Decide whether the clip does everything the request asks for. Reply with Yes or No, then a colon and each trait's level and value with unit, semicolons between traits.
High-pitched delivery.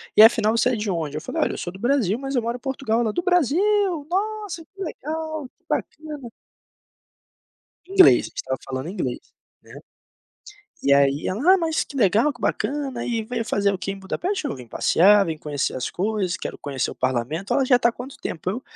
Yes: high, 235 Hz